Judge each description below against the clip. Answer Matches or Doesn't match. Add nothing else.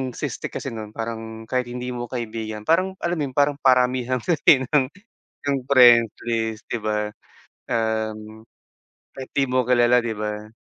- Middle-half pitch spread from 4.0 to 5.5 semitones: Doesn't match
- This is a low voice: Matches